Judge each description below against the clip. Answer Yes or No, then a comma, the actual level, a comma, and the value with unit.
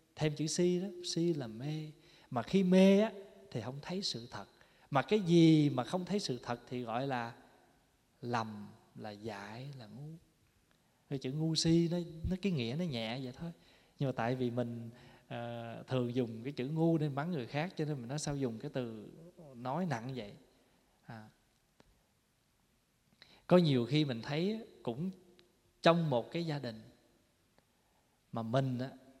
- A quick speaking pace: No, average, 175 wpm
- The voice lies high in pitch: No, low, 135 Hz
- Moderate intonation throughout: No, wide, 5.9 semitones